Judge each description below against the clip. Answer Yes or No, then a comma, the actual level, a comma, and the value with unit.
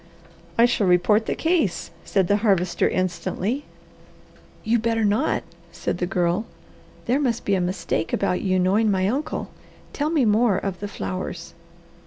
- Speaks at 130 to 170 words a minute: Yes, average, 155 wpm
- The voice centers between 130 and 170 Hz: No, high, 205 Hz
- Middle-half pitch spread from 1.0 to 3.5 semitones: No, average, 4.0 semitones